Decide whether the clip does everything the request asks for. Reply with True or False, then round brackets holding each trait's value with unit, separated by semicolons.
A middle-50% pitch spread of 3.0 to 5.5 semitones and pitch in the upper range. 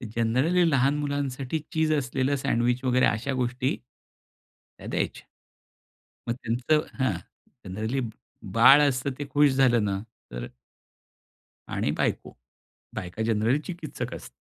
False (3.4 semitones; 130 Hz)